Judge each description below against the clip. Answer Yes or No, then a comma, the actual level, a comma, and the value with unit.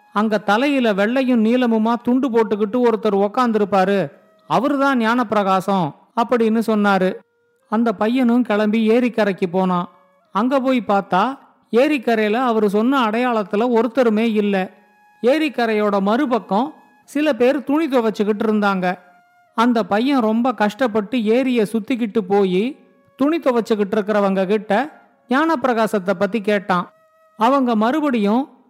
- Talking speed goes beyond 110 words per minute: No, average, 105 wpm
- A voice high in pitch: Yes, high, 225 Hz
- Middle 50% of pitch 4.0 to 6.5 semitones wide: No, average, 3.5 semitones